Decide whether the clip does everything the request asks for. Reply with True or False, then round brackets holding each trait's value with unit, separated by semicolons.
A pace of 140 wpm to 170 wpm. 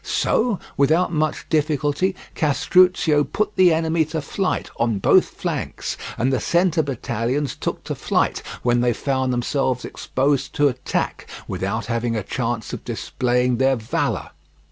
True (145 wpm)